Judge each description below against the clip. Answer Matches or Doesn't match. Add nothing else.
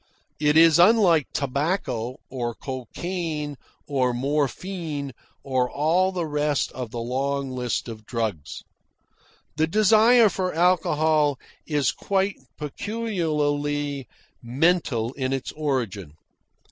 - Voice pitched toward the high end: Doesn't match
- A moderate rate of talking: Doesn't match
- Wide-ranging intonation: Doesn't match